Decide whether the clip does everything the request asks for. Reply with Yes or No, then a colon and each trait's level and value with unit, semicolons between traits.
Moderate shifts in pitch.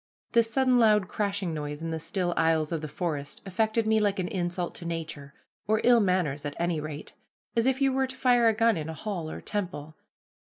No: wide, 5.7 semitones